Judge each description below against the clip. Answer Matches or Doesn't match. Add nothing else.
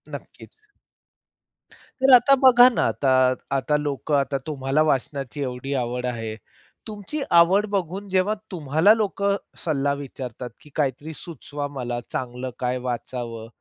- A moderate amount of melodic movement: Doesn't match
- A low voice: Doesn't match